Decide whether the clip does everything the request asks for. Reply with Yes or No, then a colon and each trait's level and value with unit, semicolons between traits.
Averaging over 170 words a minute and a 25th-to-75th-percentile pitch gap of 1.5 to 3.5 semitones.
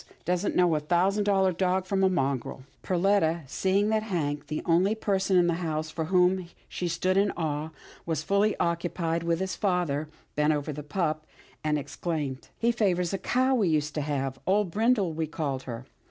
No: average, 190 wpm; average, 3.9 semitones